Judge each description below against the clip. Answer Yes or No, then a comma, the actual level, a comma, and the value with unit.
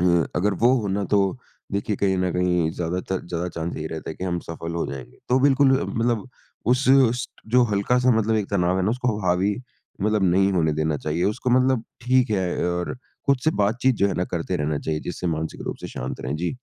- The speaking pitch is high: No, very low, 95 Hz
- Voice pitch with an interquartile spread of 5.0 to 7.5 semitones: Yes, average, 5.3 semitones